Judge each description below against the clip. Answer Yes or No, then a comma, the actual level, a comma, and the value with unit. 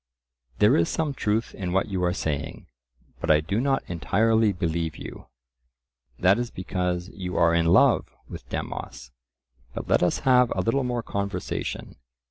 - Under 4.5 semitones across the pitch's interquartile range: No, average, 5.1 semitones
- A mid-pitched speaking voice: No, very low, 95 Hz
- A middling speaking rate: Yes, average, 160 wpm